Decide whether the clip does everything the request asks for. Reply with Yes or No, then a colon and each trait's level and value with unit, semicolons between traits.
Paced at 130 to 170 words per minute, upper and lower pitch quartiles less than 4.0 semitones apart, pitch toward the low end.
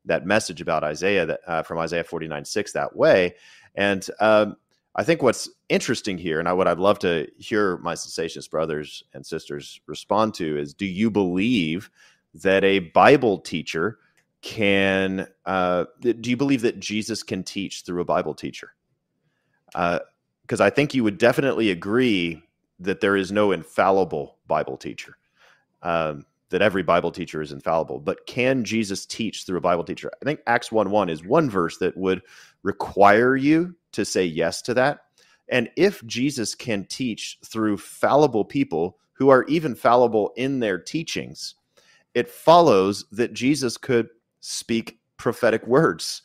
No: average, 160 wpm; average, 4.4 semitones; low, 100 Hz